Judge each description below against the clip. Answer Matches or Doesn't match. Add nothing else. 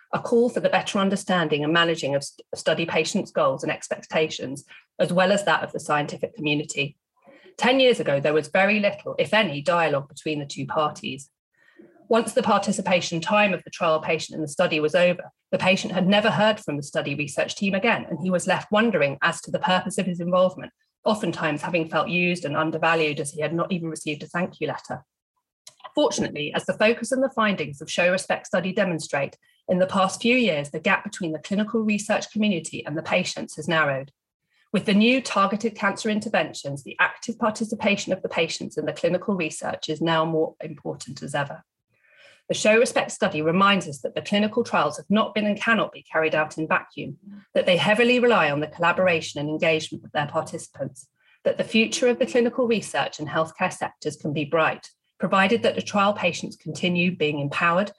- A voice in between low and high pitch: Matches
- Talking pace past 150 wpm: Matches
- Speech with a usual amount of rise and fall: Matches